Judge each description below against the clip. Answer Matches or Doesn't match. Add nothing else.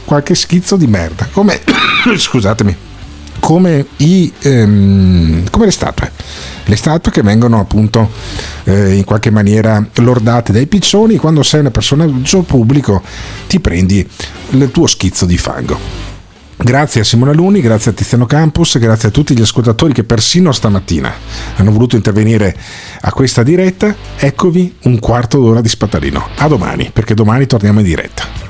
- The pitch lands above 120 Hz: Doesn't match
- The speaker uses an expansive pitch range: Matches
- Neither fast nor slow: Matches